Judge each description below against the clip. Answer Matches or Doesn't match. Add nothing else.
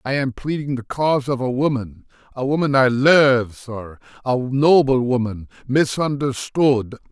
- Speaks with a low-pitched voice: Matches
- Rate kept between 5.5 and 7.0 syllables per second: Doesn't match